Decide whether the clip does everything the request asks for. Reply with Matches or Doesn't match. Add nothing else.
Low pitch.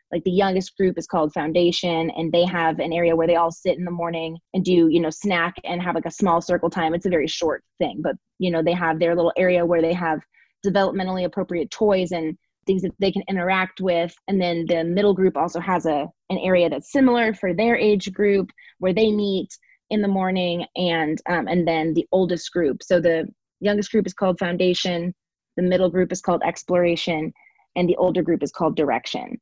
Doesn't match